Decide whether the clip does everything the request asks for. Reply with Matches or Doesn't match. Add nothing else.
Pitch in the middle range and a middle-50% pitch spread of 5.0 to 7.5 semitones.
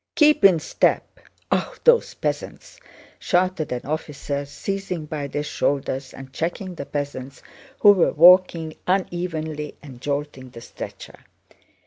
Doesn't match